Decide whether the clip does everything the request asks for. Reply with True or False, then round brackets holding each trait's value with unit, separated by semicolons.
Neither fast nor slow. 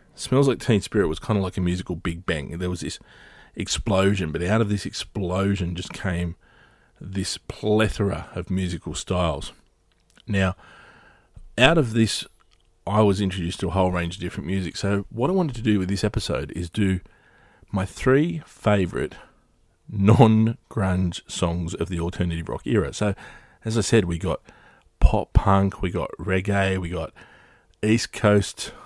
True (165 wpm)